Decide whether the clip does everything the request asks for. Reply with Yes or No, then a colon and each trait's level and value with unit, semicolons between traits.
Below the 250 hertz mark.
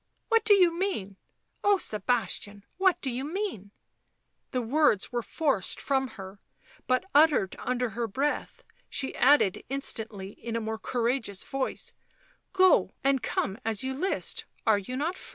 No: very high, 255 Hz